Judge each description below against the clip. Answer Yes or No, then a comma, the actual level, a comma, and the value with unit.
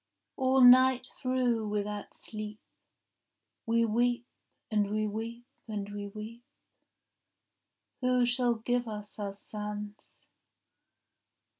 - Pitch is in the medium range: No, high, 225 Hz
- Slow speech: Yes, slow, 105 wpm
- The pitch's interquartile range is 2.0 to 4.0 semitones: Yes, average, 2.7 semitones